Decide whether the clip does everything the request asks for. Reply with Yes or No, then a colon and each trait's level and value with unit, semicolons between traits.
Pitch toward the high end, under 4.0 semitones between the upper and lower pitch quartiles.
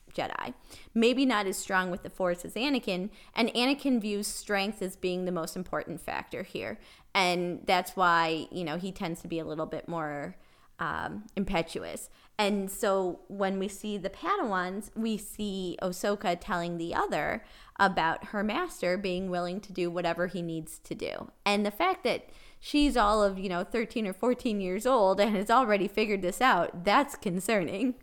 Yes: high, 195 Hz; average, 3.1 semitones